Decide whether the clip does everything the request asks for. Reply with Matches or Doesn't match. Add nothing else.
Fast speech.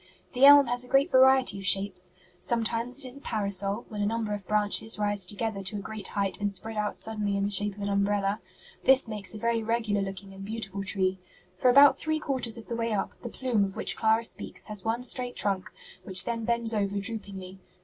Matches